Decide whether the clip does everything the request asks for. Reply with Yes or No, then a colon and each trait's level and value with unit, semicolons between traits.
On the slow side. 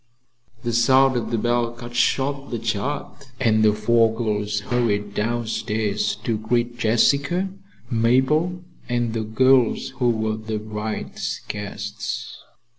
Yes: slow, 125 wpm